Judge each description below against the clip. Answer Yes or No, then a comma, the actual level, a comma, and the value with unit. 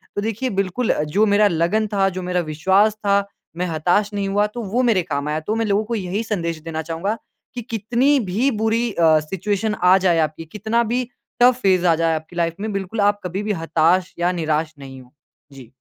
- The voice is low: No, high, 195 Hz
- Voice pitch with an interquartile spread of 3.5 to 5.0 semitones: Yes, average, 4.6 semitones